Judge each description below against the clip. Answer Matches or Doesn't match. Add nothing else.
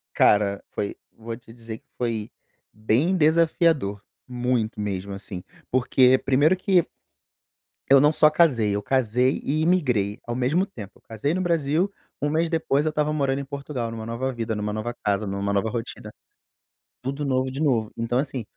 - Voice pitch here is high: Doesn't match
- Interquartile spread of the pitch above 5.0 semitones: Matches